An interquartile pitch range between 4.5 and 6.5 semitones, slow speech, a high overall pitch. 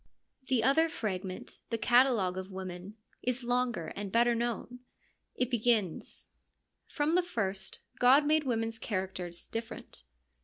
Yes: average, 4.8 semitones; slow, 125 wpm; high, 230 Hz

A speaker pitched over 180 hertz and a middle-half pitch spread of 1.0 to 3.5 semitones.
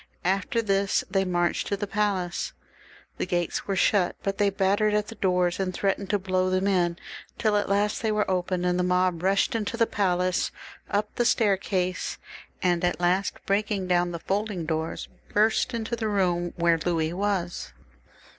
Yes: high, 190 Hz; narrow, 2.5 semitones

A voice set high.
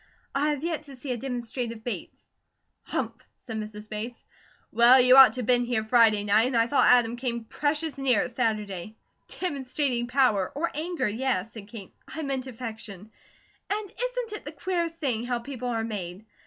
Yes: high, 245 Hz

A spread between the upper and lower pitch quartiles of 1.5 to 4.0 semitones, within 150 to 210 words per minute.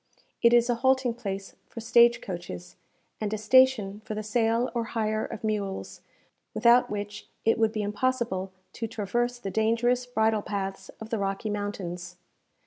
Yes: average, 2.9 semitones; average, 160 wpm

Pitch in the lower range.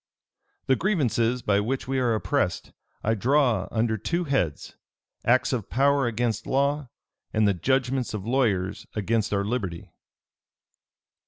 Yes: low, 120 Hz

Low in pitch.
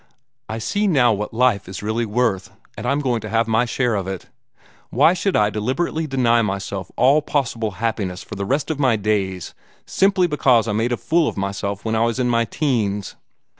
Yes: low, 115 Hz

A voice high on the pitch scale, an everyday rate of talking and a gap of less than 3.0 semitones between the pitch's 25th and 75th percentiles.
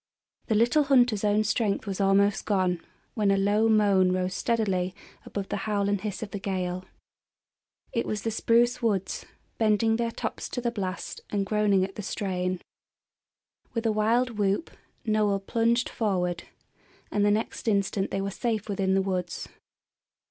Yes: high, 205 Hz; average, 165 wpm; narrow, 2.5 semitones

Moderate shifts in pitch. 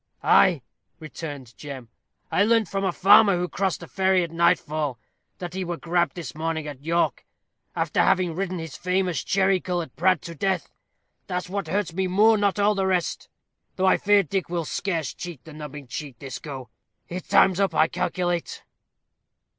Yes: average, 3.3 semitones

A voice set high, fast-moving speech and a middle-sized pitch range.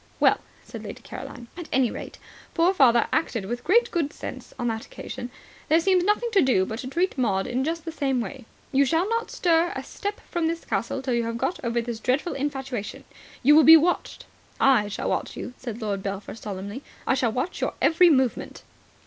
No: very high, 265 Hz; fast, 210 wpm; wide, 6.1 semitones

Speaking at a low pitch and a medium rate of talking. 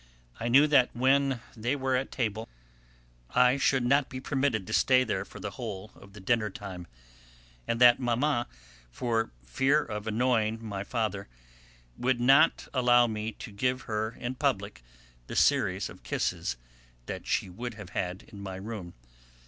Yes: low, 120 Hz; average, 160 wpm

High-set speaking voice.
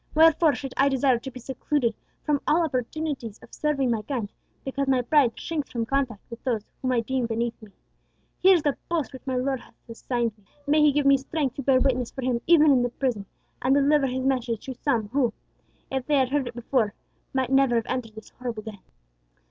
Yes: very high, 260 Hz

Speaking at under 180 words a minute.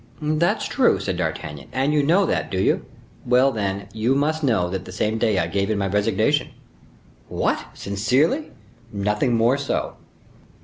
Yes: average, 165 wpm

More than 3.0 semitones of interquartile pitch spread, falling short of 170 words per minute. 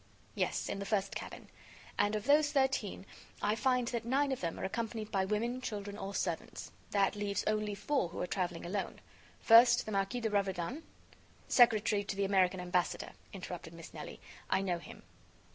No: average, 3.5 semitones; average, 180 wpm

